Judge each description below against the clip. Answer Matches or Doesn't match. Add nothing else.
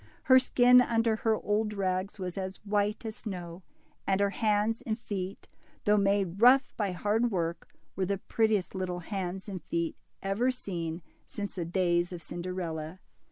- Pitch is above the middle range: Matches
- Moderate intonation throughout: Matches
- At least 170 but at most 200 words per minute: Doesn't match